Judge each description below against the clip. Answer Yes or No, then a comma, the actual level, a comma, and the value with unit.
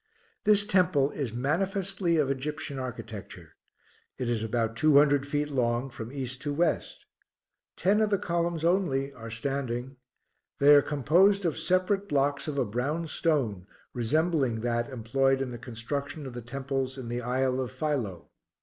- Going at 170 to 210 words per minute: No, average, 160 wpm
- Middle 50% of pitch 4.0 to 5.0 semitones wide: Yes, average, 4.4 semitones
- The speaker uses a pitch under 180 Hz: Yes, medium, 140 Hz